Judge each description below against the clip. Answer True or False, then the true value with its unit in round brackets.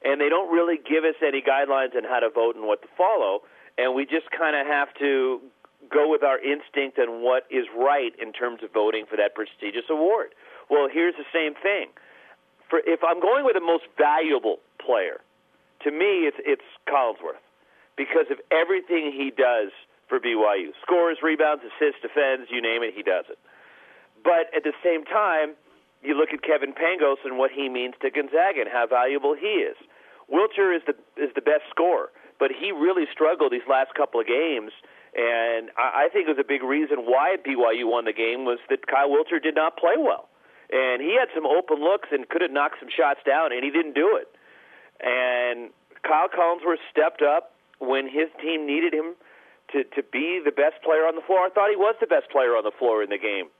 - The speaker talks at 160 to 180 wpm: False (205 wpm)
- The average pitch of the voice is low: False (155 Hz)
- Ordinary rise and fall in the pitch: False (6.9 semitones)